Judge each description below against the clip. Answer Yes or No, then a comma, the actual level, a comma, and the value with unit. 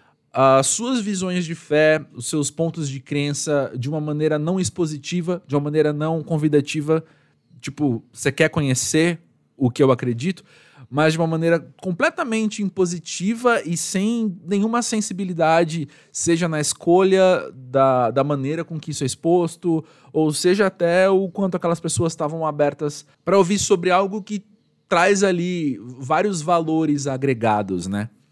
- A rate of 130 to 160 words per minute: Yes, average, 145 wpm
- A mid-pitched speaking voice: Yes, medium, 160 Hz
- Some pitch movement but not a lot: Yes, average, 4.1 semitones